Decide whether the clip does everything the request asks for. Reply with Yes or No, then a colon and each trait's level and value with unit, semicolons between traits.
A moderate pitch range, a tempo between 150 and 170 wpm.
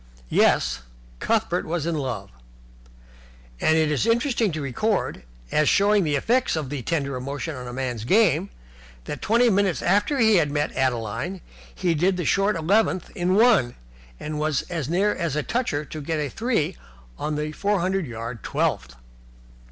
No: wide, 6.0 semitones; average, 160 wpm